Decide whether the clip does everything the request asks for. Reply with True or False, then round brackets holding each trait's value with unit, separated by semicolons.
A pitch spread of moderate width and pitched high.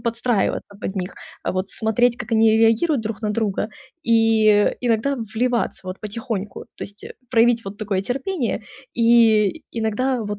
False (2.3 semitones; 225 Hz)